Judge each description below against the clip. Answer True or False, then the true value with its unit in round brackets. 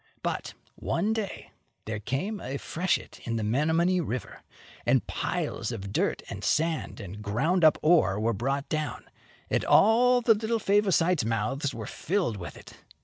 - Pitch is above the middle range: False (155 Hz)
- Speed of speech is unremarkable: True (160 wpm)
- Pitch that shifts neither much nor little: False (8.7 semitones)